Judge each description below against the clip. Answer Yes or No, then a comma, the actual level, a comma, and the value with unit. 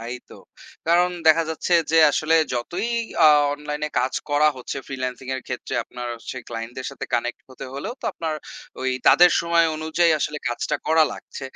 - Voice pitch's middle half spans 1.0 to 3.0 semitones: No, average, 4.2 semitones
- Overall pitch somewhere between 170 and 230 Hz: No, medium, 150 Hz